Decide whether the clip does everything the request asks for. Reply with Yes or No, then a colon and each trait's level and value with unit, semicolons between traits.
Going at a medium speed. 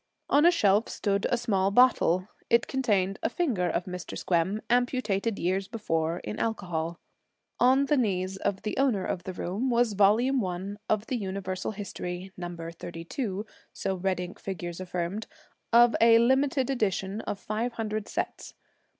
Yes: average, 160 wpm